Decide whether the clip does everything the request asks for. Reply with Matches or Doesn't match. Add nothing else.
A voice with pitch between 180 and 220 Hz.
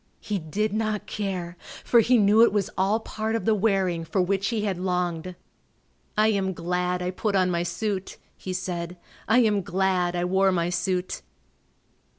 Matches